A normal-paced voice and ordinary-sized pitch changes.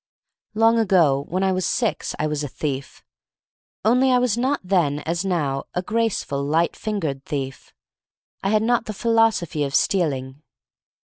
No: average, 165 wpm; wide, 7.5 semitones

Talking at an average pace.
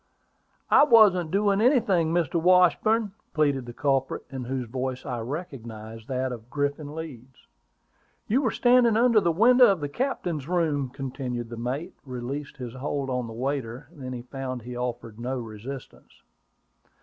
Yes: average, 160 wpm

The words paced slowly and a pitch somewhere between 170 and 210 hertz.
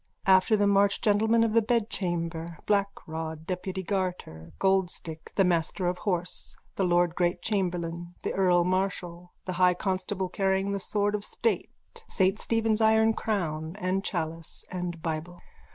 No: average, 150 wpm; medium, 185 Hz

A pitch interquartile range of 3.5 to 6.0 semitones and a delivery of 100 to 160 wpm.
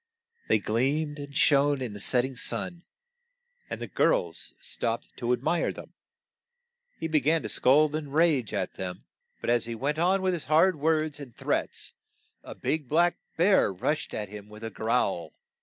No: average, 5.1 semitones; average, 190 wpm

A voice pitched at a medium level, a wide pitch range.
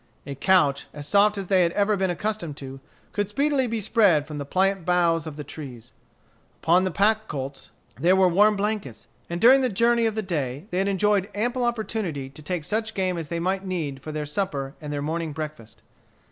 Yes: medium, 180 Hz; wide, 5.8 semitones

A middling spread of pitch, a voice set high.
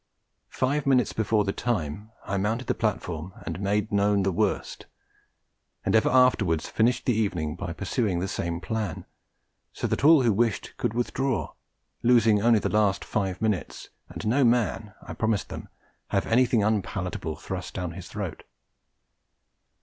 No: average, 3.6 semitones; low, 105 Hz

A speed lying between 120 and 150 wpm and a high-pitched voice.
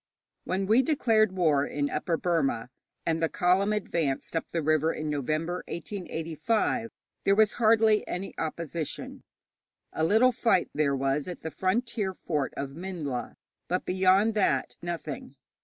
No: average, 140 wpm; medium, 175 Hz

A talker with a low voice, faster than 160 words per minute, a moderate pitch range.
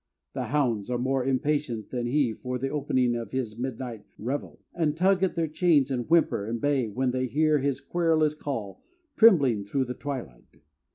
Yes: low, 130 Hz; average, 180 wpm; average, 3.8 semitones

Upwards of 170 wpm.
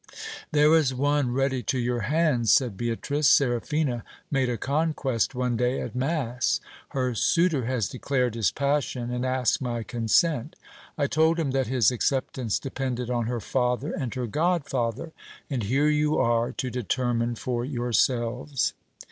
No: average, 155 wpm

